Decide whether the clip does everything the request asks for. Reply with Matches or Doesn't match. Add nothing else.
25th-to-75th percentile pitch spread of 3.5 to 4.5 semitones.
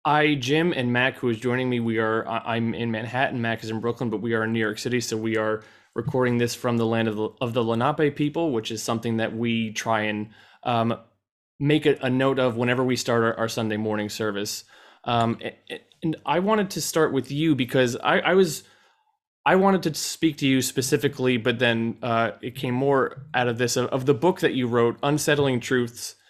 Matches